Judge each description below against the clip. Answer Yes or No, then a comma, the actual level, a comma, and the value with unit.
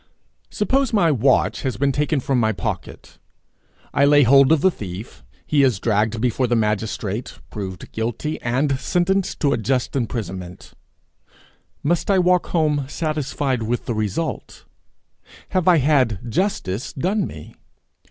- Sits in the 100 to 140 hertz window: Yes, low, 135 Hz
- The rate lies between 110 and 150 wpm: Yes, average, 145 wpm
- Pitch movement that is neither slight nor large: No, wide, 5.8 semitones